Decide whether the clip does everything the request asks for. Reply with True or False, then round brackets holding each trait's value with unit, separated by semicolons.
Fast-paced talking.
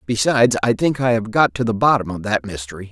True (245 wpm)